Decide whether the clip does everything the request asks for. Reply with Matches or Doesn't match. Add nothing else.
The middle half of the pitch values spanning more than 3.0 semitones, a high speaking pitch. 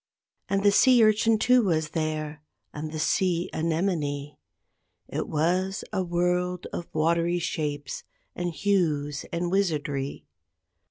Doesn't match